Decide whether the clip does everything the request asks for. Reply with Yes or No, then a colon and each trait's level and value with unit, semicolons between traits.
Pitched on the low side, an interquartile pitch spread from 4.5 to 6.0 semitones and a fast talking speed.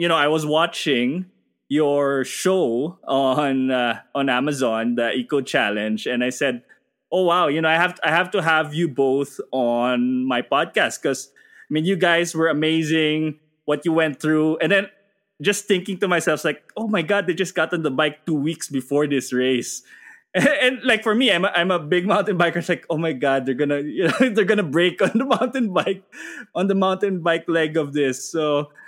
No: medium, 160 Hz; average, 4.8 semitones; fast, 210 wpm